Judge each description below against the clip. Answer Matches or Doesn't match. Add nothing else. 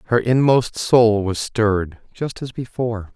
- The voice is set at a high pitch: Doesn't match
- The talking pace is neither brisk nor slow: Matches